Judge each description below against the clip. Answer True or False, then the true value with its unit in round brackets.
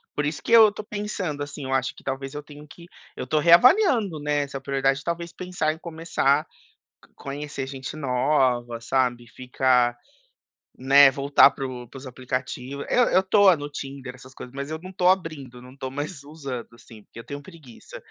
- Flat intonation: False (3.6 semitones)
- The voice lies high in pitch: False (140 Hz)